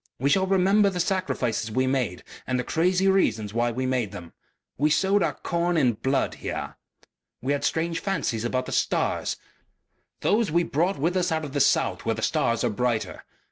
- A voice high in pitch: No, medium, 145 Hz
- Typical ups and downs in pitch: No, wide, 6.7 semitones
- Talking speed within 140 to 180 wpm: No, average, 190 wpm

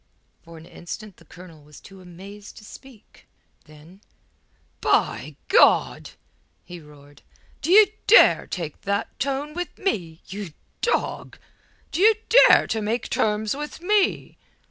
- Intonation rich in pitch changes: Yes, wide, 8.7 semitones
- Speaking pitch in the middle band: No, high, 205 Hz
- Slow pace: Yes, slow, 125 wpm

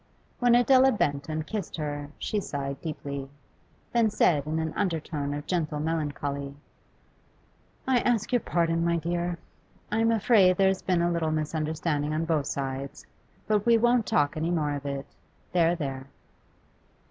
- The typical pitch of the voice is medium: Yes, medium, 160 Hz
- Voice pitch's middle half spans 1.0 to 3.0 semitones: No, average, 4.7 semitones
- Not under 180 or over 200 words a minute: No, average, 160 wpm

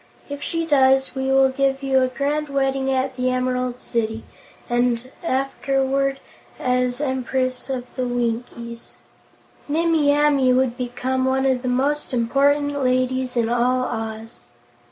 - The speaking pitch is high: Yes, very high, 260 Hz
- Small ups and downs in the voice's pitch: Yes, narrow, 1.6 semitones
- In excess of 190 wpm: No, slow, 135 wpm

